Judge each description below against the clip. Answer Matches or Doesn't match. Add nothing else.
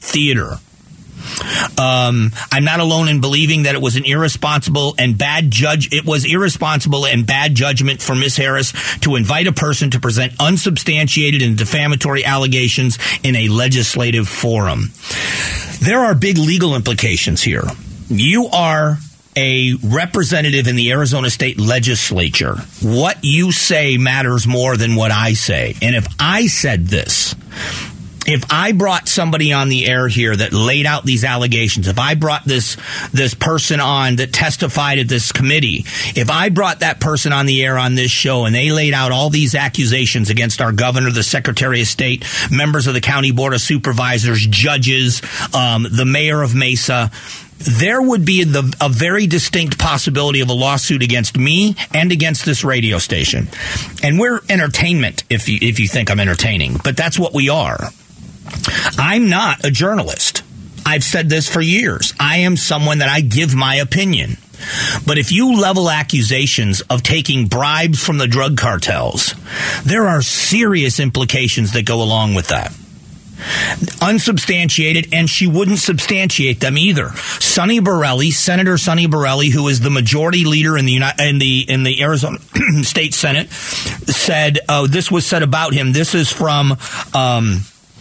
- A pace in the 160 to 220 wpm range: Matches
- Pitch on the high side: Doesn't match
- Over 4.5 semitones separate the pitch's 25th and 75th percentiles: Doesn't match